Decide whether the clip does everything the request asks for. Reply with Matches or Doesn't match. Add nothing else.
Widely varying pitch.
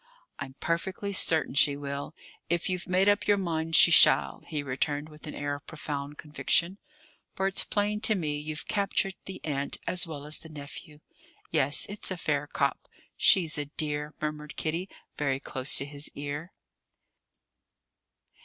Doesn't match